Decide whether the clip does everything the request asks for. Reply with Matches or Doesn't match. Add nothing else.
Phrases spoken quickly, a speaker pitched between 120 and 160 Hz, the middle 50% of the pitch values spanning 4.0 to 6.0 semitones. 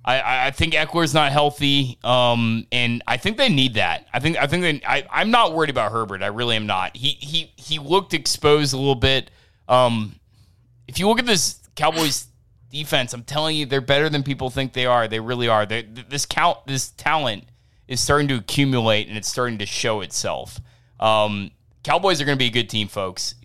Matches